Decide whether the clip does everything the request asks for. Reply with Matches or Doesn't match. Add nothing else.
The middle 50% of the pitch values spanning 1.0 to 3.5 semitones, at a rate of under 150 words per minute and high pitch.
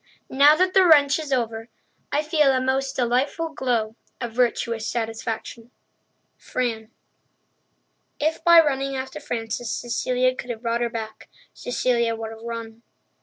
Matches